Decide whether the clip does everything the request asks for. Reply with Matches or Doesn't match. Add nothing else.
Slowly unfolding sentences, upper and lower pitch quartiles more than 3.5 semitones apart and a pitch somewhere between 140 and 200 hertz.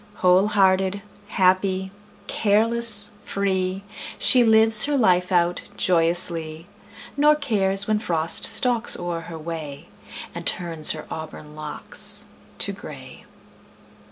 Matches